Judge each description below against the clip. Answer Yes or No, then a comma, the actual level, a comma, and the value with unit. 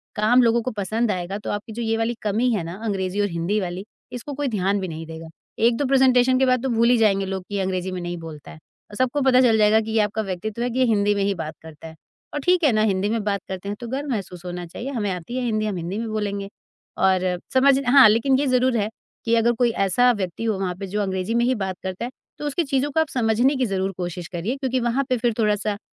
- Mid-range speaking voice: No, high, 215 Hz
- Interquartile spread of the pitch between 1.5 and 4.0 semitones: No, average, 4.6 semitones